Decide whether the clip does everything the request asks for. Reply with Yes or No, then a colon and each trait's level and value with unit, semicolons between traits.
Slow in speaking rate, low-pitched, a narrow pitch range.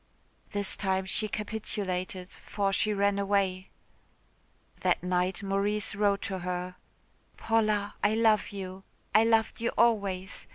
No: slow, 125 wpm; high, 200 Hz; narrow, 2.0 semitones